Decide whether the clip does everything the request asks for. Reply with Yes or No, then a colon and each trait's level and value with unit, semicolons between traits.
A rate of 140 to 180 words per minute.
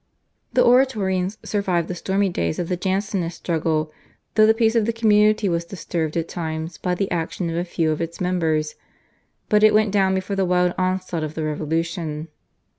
No: average, 190 wpm